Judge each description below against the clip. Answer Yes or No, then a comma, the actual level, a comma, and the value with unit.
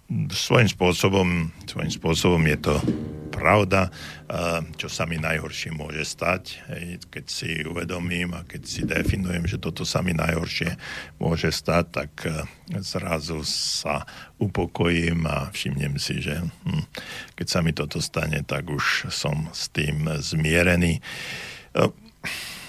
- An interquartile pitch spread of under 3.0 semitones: Yes, narrow, 2.4 semitones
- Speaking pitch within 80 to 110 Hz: Yes, very low, 85 Hz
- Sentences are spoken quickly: No, average, 120 wpm